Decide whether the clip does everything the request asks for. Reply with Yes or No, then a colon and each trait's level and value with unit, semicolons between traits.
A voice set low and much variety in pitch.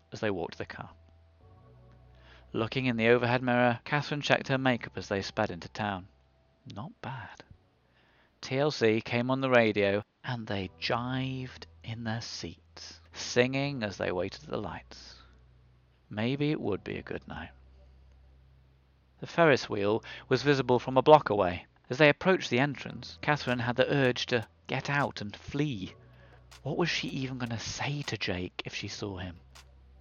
Yes: low, 105 Hz; wide, 8.9 semitones